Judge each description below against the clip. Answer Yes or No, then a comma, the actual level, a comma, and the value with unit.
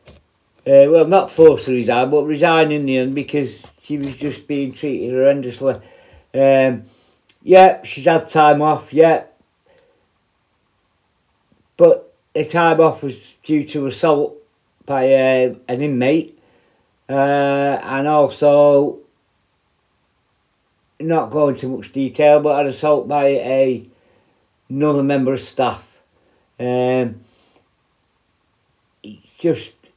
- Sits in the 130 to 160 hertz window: Yes, medium, 140 Hz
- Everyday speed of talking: No, slow, 115 wpm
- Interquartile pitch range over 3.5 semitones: No, average, 3.0 semitones